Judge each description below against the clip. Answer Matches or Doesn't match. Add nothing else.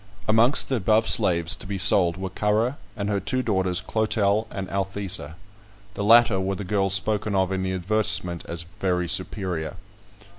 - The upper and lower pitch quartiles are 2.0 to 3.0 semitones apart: Matches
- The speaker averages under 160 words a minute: Doesn't match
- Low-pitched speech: Matches